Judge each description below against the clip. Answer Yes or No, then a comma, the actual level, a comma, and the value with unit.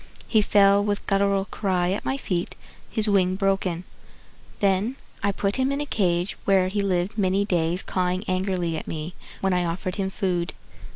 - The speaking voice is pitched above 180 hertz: Yes, high, 190 Hz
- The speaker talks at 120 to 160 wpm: No, average, 175 wpm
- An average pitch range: No, narrow, 2.0 semitones